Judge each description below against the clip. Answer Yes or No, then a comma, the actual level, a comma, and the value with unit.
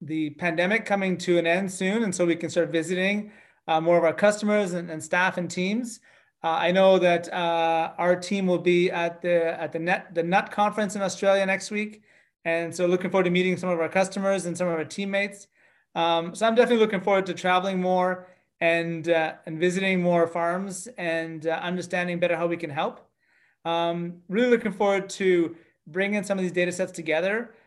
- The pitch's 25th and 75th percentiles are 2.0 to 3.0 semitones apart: Yes, narrow, 2.5 semitones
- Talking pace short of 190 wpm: No, fast, 205 wpm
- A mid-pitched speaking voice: Yes, medium, 180 Hz